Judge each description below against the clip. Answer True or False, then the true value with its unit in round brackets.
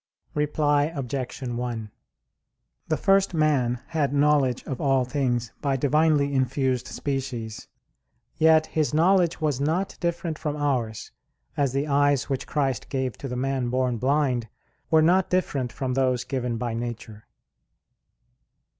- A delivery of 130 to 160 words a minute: True (135 wpm)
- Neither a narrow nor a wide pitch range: True (3.3 semitones)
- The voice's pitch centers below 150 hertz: True (135 Hz)